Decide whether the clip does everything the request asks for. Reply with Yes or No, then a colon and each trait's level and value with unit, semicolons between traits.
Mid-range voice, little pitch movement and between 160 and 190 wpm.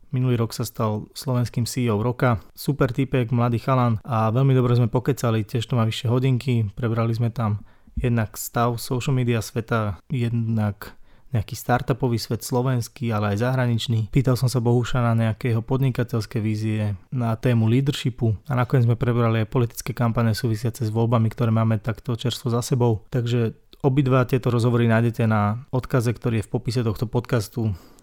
No: low, 120 Hz; narrow, 2.0 semitones; fast, 165 wpm